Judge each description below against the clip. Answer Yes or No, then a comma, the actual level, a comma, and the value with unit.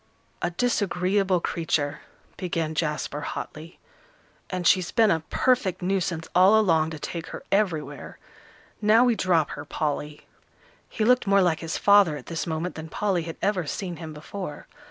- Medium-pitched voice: Yes, medium, 175 Hz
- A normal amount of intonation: Yes, average, 3.8 semitones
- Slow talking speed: No, average, 155 wpm